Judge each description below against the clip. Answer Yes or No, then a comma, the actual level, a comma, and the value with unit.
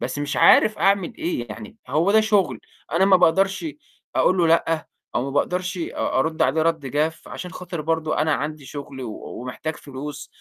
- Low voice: No, medium, 160 Hz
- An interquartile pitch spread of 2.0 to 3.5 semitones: No, average, 4.0 semitones